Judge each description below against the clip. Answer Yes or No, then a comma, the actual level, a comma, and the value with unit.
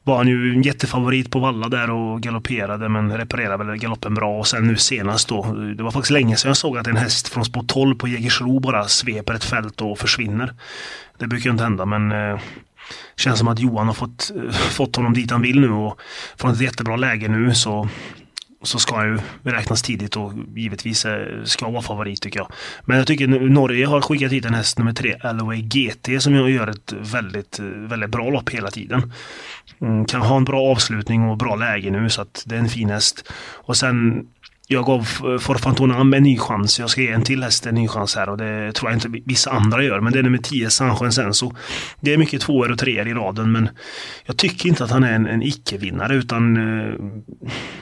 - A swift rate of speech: Yes, fast, 220 wpm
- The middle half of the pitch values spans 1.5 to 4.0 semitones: Yes, average, 2.9 semitones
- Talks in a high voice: No, low, 115 Hz